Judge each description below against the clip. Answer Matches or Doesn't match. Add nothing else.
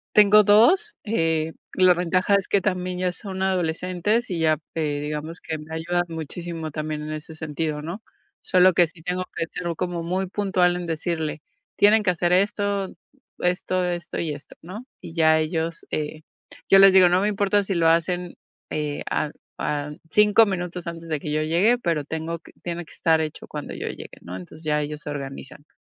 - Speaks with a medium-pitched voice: Matches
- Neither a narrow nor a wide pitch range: Matches